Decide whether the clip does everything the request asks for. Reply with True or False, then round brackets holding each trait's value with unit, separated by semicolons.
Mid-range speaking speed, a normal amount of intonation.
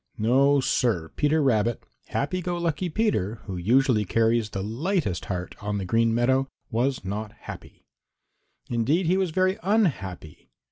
False (145 wpm; 7.3 semitones)